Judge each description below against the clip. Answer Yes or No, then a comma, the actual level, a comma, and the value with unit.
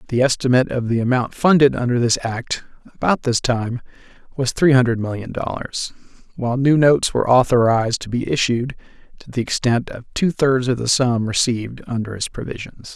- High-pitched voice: No, low, 125 Hz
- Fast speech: No, average, 175 wpm